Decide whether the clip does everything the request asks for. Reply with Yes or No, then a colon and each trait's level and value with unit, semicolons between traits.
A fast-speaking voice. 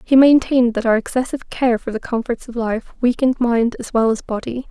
Yes: fast, 215 wpm